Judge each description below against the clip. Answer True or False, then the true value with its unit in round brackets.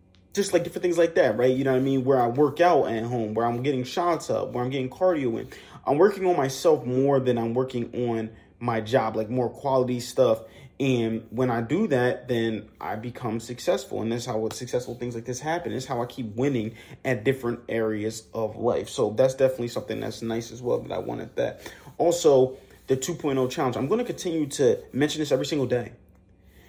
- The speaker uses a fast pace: True (215 wpm)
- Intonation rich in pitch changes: False (3.0 semitones)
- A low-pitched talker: True (125 Hz)